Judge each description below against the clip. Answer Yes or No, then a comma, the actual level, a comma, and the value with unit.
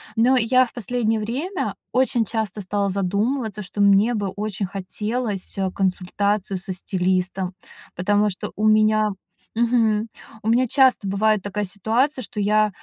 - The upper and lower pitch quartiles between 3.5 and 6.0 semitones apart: No, average, 2.7 semitones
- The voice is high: Yes, high, 210 Hz